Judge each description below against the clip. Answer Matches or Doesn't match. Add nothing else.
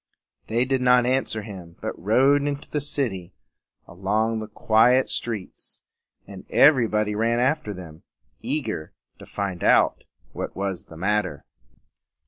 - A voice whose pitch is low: Matches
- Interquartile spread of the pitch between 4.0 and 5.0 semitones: Matches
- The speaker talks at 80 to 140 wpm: Matches